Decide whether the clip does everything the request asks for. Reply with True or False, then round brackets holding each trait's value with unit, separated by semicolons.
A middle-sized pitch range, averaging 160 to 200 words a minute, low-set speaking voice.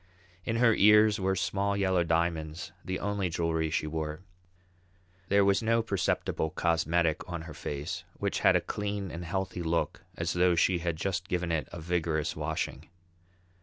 True (3.3 semitones; 165 wpm; 90 Hz)